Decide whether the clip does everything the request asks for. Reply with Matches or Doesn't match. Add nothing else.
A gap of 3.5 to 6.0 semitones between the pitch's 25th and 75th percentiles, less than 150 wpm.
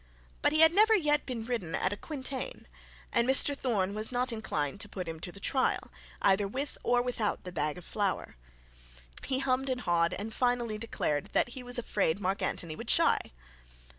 Doesn't match